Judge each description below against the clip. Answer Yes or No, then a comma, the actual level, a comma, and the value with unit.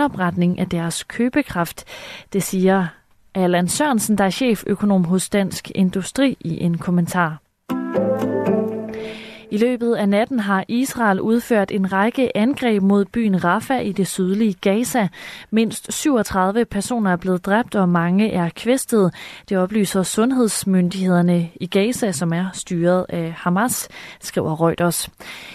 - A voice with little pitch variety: No, average, 3.6 semitones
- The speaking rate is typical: No, slow, 130 wpm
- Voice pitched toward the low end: No, high, 195 Hz